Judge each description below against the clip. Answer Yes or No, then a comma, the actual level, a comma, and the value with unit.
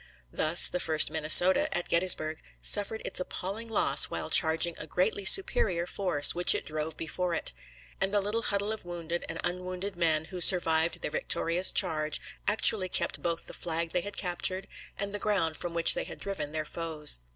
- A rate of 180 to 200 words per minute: Yes, average, 185 wpm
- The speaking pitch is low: No, medium, 175 Hz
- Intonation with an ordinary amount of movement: Yes, average, 3.1 semitones